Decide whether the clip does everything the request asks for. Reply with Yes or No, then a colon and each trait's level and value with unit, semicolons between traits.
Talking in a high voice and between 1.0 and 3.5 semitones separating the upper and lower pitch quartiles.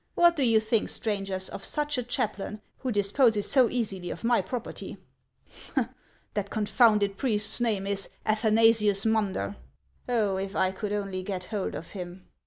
Yes: high, 210 Hz; average, 2.7 semitones